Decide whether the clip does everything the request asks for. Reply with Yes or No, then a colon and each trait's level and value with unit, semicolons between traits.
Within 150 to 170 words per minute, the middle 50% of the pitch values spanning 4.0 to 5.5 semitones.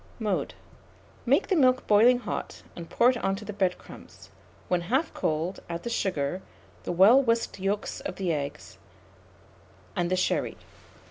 Yes: average, 160 wpm; average, 5.1 semitones